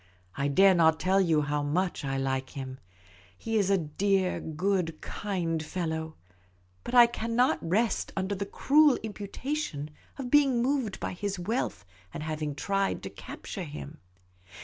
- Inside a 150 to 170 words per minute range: Yes, average, 155 wpm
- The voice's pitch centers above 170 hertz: Yes, medium, 185 Hz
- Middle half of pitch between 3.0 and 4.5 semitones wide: No, average, 5.2 semitones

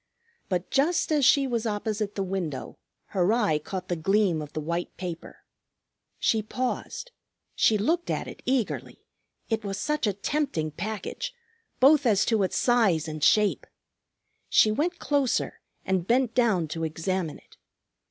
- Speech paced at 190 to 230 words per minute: No, average, 150 wpm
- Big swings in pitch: Yes, wide, 6.0 semitones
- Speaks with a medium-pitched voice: No, high, 210 Hz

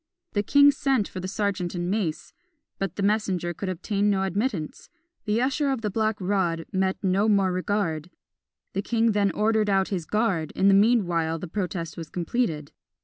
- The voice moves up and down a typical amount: Yes, average, 3.3 semitones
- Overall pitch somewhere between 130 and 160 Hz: No, high, 195 Hz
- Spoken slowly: No, average, 180 wpm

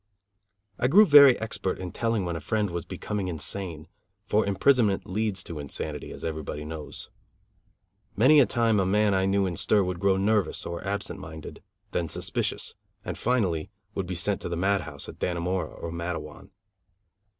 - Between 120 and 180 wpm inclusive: Yes, average, 170 wpm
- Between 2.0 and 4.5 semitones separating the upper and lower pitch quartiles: Yes, average, 4.0 semitones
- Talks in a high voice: No, very low, 95 Hz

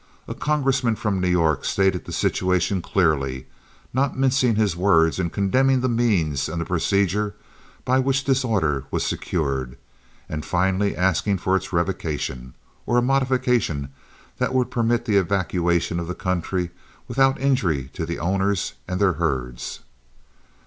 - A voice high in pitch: No, very low, 95 Hz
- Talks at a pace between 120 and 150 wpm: Yes, average, 145 wpm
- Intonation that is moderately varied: No, wide, 6.3 semitones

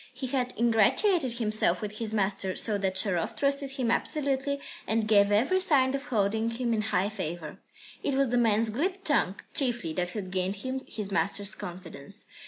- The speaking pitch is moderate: No, high, 220 Hz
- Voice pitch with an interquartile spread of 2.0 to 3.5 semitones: No, average, 5.1 semitones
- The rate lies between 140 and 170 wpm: No, average, 180 wpm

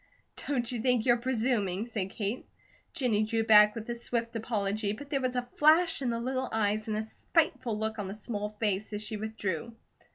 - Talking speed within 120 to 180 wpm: No, average, 200 wpm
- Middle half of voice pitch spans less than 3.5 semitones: Yes, average, 2.7 semitones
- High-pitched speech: Yes, high, 225 Hz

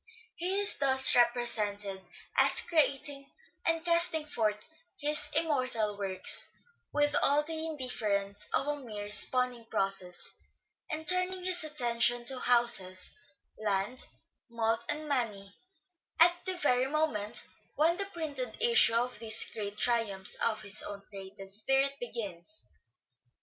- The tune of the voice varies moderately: No, wide, 6.4 semitones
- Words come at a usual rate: No, slow, 130 wpm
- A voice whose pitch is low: No, high, 245 Hz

